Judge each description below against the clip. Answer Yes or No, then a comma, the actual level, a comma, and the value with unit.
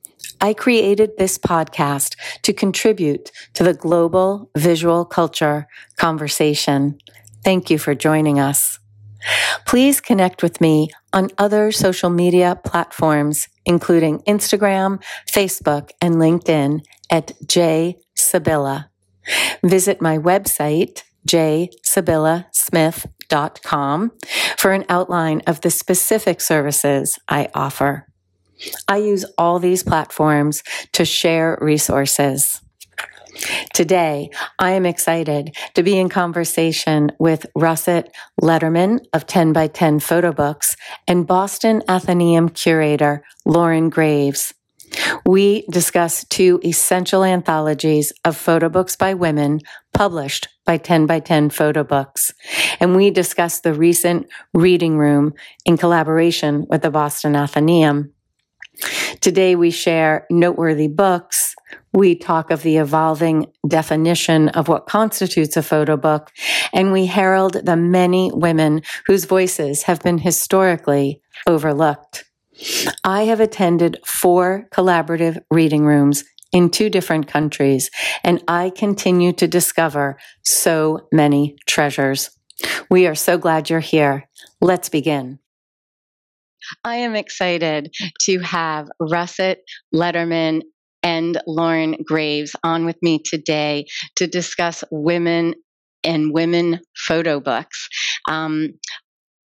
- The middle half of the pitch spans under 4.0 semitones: Yes, average, 2.9 semitones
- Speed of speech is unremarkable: No, slow, 110 wpm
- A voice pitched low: No, medium, 165 Hz